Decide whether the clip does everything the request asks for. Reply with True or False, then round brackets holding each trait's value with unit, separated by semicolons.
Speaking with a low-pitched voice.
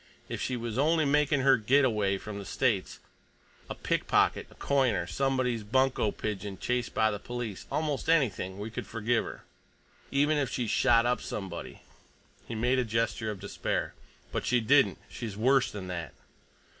True (120 Hz)